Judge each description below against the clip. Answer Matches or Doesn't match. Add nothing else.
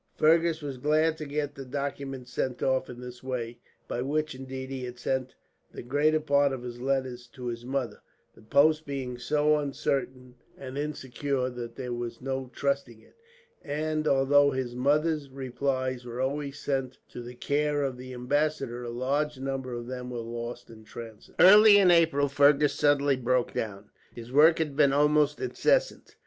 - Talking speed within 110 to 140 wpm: Doesn't match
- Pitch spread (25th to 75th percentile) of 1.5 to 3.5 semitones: Matches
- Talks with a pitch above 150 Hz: Doesn't match